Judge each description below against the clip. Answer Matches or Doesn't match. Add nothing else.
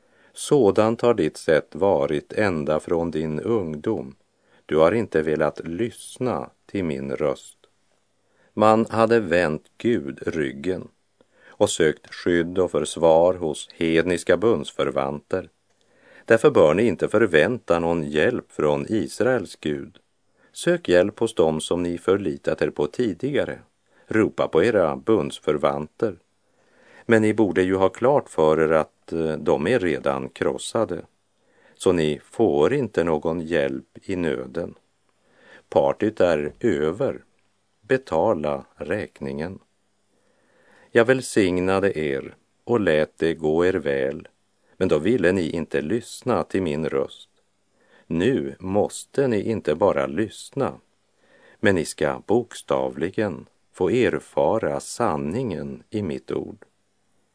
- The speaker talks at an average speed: Doesn't match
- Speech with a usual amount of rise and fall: Matches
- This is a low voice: Matches